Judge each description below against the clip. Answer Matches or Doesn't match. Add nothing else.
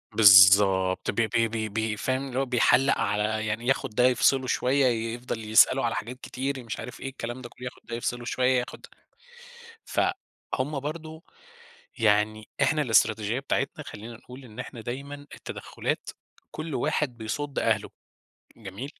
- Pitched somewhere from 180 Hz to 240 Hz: Doesn't match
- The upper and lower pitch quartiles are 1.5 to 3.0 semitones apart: Doesn't match